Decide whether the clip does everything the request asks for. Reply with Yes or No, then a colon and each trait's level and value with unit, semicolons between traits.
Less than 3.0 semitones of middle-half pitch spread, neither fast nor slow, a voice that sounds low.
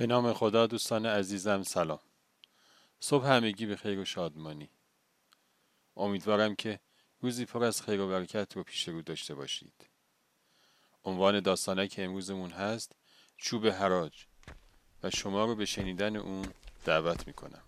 Yes: narrow, 2.6 semitones; average, 135 wpm; low, 100 Hz